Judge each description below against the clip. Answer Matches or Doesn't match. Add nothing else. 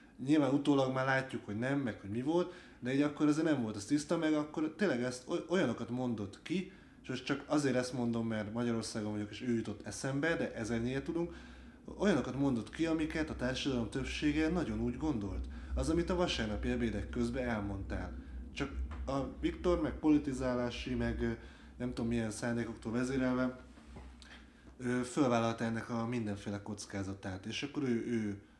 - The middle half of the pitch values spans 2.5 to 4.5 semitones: Doesn't match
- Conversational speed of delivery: Doesn't match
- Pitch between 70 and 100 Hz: Doesn't match